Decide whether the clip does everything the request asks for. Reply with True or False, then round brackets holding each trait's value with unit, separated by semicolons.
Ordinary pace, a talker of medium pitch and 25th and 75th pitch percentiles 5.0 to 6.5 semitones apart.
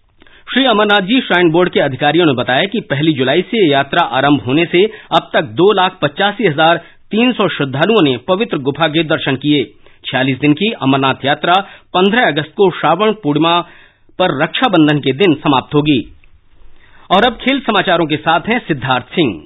True (175 wpm; 170 Hz; 5.4 semitones)